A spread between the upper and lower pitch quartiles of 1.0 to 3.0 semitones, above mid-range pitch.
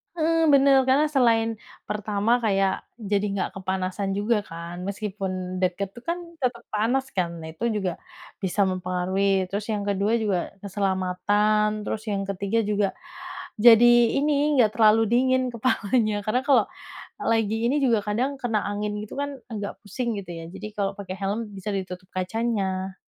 No: average, 3.4 semitones; high, 210 Hz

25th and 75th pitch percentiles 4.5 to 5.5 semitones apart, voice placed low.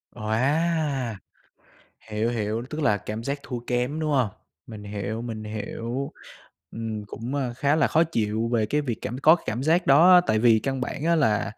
Yes: average, 4.8 semitones; low, 120 Hz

